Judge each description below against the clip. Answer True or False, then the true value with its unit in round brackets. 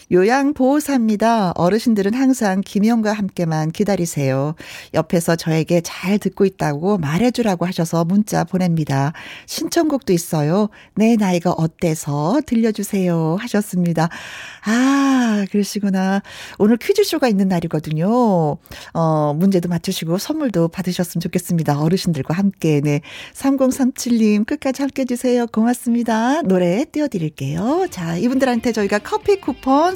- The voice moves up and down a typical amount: False (6.1 semitones)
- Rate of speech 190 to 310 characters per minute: False (320 characters per minute)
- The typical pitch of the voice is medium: False (200 Hz)